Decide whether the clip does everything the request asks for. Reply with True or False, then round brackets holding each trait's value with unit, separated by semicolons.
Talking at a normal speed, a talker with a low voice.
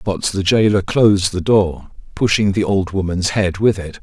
True (195 wpm; 100 Hz)